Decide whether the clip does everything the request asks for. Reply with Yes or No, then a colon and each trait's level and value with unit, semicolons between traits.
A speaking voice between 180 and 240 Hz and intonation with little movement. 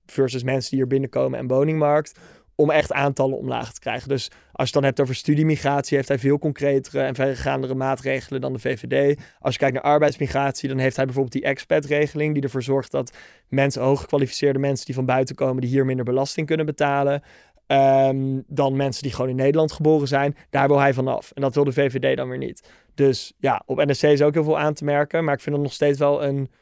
No: medium, 140 Hz; narrow, 1.5 semitones